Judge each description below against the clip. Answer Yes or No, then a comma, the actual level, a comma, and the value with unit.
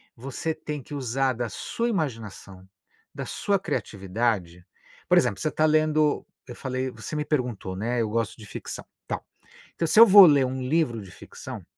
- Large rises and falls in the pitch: Yes, wide, 5.8 semitones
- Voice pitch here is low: Yes, low, 130 Hz